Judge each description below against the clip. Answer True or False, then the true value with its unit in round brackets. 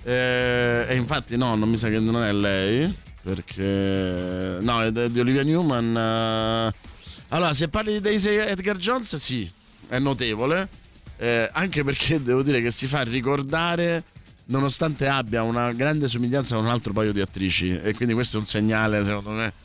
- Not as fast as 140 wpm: False (170 wpm)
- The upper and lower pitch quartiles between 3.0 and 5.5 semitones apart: True (4.6 semitones)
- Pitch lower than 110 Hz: False (120 Hz)